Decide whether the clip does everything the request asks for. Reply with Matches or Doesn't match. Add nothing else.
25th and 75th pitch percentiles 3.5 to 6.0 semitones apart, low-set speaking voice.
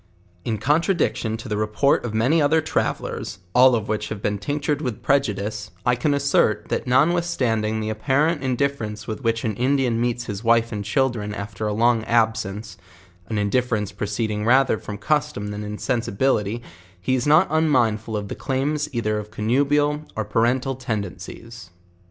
Matches